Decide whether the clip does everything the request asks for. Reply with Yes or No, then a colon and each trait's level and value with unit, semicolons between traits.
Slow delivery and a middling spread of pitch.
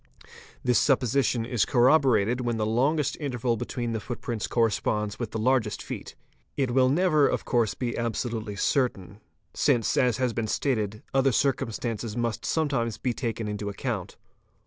No: average, 155 wpm; average, 3.0 semitones